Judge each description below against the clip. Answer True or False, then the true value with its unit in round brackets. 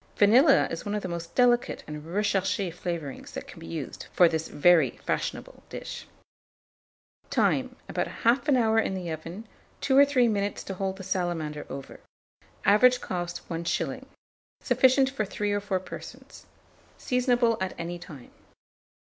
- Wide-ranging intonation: True (5.8 semitones)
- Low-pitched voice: False (195 Hz)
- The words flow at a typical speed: True (150 wpm)